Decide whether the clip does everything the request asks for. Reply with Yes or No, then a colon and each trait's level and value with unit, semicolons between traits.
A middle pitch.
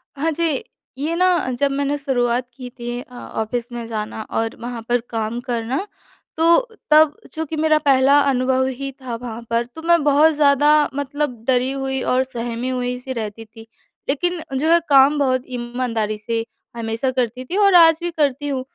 No: very high, 260 Hz